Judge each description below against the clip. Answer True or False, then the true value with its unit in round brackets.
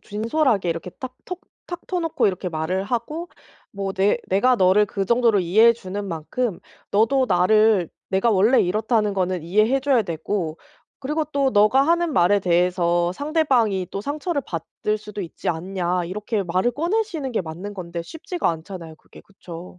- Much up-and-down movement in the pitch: True (5.9 semitones)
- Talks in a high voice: True (205 Hz)